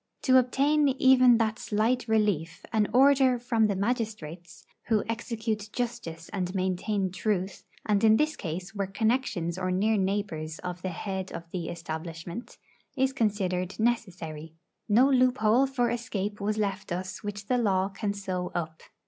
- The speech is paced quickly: No, average, 150 wpm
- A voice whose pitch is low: No, high, 205 Hz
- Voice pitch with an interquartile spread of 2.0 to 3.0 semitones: No, average, 4.3 semitones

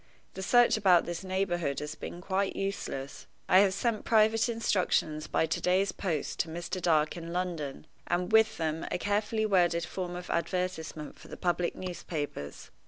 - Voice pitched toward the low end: No, medium, 180 Hz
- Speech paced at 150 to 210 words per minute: Yes, average, 170 wpm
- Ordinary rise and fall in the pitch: Yes, average, 3.3 semitones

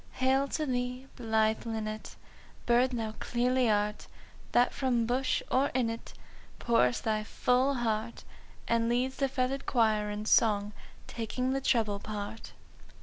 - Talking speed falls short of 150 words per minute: Yes, average, 140 wpm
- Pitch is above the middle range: Yes, high, 235 Hz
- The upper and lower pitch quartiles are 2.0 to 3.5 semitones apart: Yes, average, 2.9 semitones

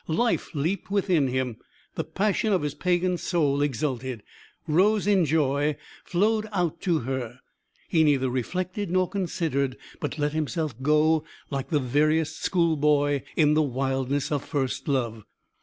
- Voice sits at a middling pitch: Yes, medium, 150 Hz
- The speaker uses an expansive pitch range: No, average, 4.4 semitones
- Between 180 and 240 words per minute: No, average, 140 wpm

